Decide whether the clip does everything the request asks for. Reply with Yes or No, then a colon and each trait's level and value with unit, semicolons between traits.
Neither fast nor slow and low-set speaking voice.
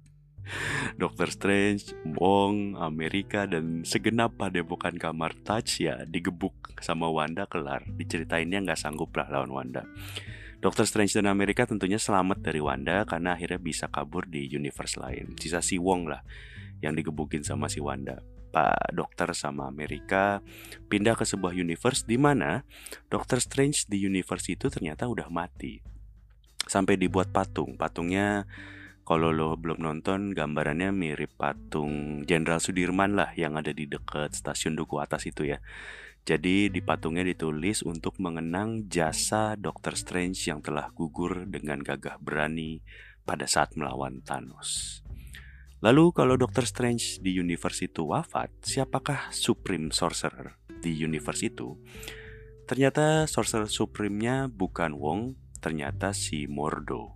Yes: average, 130 wpm; very low, 90 Hz